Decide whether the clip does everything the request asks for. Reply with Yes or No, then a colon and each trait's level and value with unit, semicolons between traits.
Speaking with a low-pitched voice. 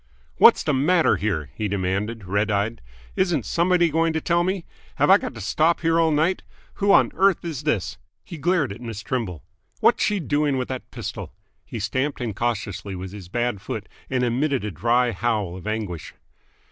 Yes: low, 120 Hz